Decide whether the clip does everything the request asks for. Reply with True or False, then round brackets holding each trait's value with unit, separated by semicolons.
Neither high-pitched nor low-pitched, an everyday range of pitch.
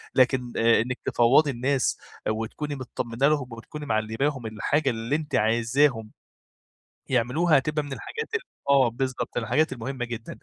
False (130 Hz; 3.8 semitones)